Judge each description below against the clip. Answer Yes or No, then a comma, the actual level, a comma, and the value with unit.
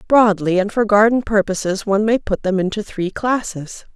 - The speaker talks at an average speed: Yes, average, 180 wpm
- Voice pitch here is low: No, high, 205 Hz